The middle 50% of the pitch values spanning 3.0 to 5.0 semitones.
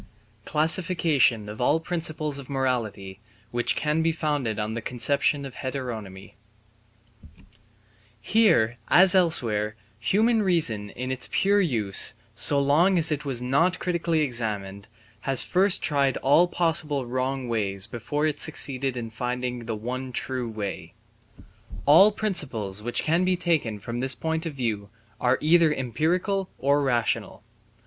No: wide, 5.6 semitones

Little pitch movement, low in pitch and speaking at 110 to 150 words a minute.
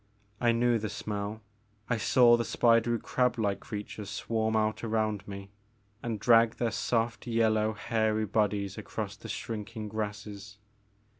Yes: narrow, 1.8 semitones; low, 110 Hz; average, 140 wpm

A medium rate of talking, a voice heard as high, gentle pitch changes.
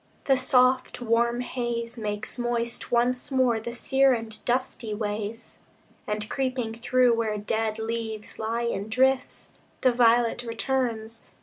No: slow, 130 wpm; high, 235 Hz; narrow, 2.1 semitones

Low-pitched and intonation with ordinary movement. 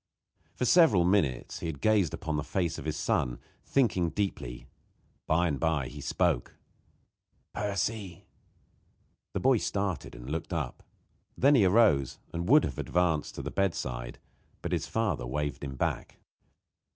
No: very low, 85 Hz; wide, 5.8 semitones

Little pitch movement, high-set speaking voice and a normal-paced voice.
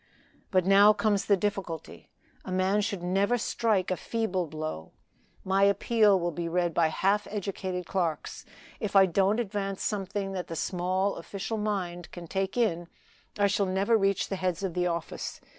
Yes: narrow, 2.3 semitones; high, 195 Hz; average, 170 wpm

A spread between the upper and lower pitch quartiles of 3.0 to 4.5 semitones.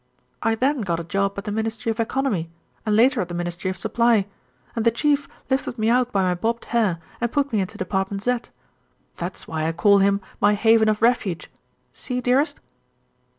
Yes: average, 3.8 semitones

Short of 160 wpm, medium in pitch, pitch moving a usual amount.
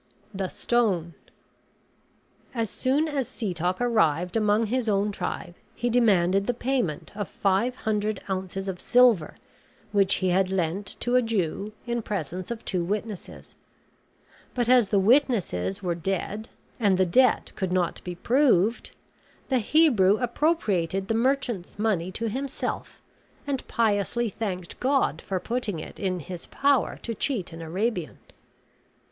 No: average, 140 wpm; high, 205 Hz; average, 4.6 semitones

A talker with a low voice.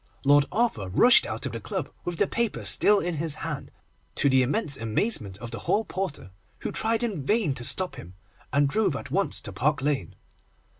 No: medium, 145 Hz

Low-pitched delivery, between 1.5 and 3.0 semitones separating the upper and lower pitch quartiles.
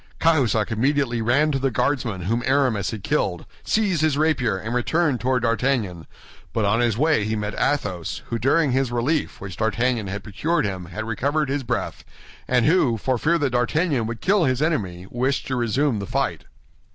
No: low, 125 Hz; average, 4.8 semitones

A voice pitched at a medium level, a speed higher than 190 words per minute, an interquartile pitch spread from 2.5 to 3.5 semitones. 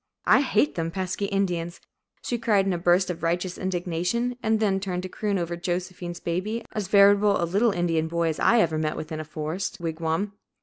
Yes: medium, 180 Hz; fast, 205 wpm; average, 3.0 semitones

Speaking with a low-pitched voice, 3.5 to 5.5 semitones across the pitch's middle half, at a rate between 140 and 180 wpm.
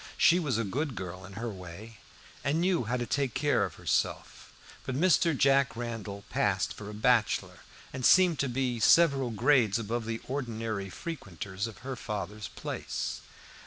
Yes: low, 120 Hz; average, 4.6 semitones; average, 165 wpm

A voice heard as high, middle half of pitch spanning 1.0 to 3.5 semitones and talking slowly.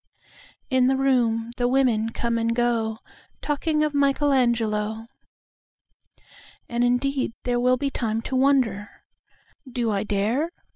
Yes: high, 245 Hz; average, 3.0 semitones; slow, 105 wpm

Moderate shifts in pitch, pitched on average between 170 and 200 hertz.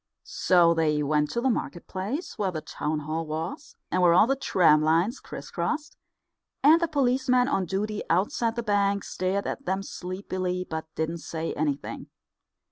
No: wide, 6.3 semitones; medium, 185 Hz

